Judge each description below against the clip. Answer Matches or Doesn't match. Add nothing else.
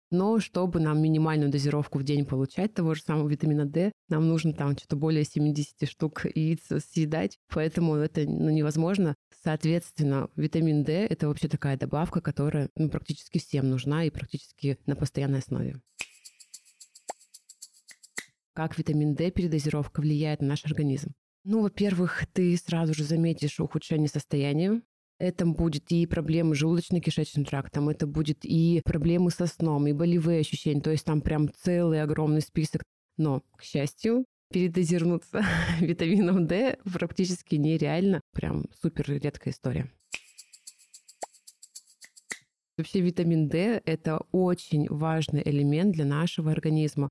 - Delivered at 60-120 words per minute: Doesn't match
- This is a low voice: Doesn't match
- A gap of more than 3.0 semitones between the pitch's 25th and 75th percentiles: Doesn't match